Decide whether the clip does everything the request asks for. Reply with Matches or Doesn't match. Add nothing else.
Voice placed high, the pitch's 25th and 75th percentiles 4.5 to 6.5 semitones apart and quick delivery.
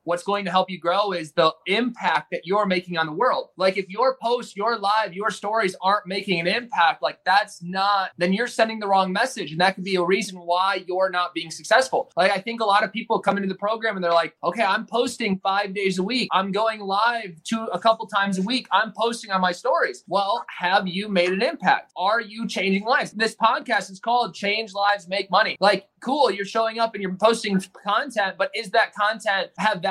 Doesn't match